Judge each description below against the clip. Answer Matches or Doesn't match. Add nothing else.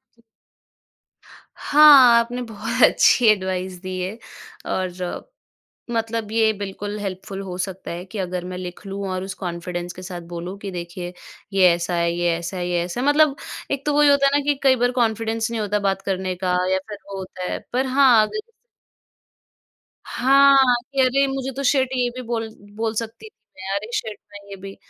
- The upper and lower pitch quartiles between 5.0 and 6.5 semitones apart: Matches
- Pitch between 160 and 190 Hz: Doesn't match